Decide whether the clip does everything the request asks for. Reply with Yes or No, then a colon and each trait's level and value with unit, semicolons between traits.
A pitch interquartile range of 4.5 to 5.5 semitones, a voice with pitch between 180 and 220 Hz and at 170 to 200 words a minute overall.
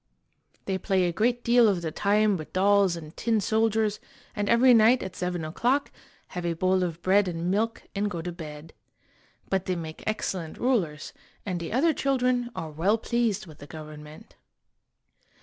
Yes: average, 4.9 semitones; high, 190 Hz; average, 175 wpm